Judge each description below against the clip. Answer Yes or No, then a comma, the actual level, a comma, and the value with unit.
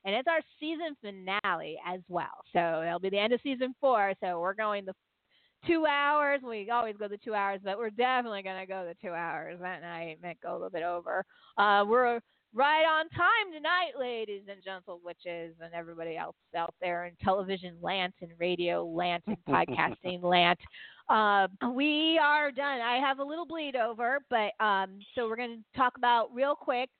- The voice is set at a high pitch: Yes, high, 205 Hz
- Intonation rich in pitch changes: Yes, wide, 6.3 semitones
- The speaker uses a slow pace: No, average, 195 wpm